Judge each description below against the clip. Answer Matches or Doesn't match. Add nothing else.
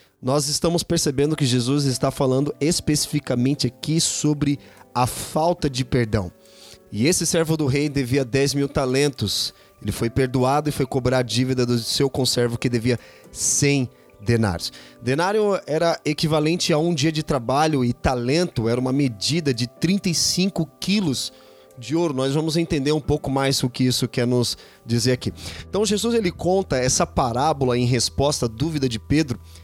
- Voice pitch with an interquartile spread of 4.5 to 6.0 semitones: Doesn't match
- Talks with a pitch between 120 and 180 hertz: Matches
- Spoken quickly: Doesn't match